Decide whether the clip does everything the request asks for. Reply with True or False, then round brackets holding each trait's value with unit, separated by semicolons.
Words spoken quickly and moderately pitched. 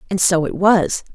True (210 wpm; 180 Hz)